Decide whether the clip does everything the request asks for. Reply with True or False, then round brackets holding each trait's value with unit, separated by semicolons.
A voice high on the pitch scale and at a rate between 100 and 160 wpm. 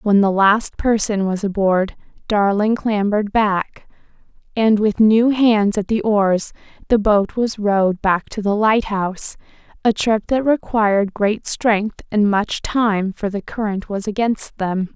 True (210 Hz; 150 wpm)